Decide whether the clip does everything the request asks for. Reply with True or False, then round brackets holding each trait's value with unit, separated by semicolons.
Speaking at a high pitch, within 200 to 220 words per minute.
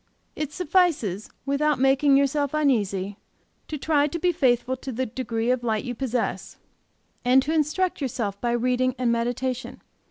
False (260 Hz; 155 wpm)